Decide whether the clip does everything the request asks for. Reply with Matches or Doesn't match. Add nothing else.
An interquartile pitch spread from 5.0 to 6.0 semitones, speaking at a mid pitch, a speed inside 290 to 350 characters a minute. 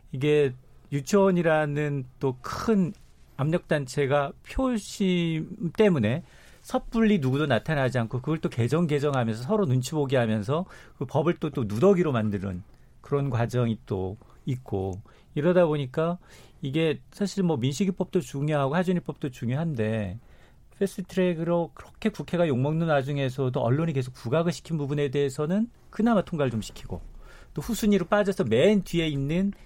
Matches